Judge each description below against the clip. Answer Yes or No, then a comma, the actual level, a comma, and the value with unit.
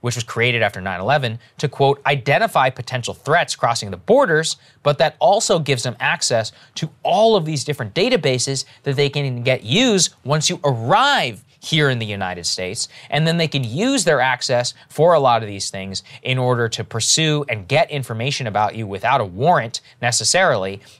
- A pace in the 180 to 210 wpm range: Yes, average, 185 wpm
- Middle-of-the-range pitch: No, low, 130 Hz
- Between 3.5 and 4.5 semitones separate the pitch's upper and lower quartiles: Yes, average, 4.2 semitones